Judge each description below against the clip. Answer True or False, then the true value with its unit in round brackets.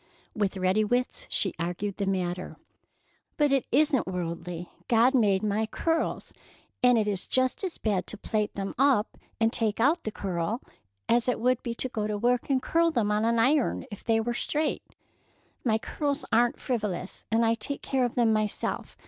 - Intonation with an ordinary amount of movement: True (3.7 semitones)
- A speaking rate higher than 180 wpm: True (190 wpm)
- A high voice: True (225 Hz)